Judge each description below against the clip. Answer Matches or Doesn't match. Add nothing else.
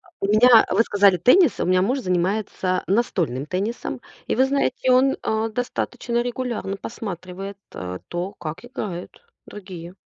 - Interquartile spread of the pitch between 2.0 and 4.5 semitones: Doesn't match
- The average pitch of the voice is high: Matches